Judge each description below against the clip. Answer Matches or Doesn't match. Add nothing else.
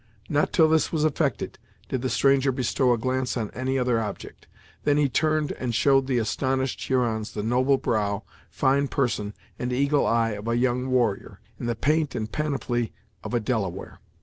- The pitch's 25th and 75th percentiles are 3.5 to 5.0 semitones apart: Doesn't match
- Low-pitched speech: Matches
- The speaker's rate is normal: Matches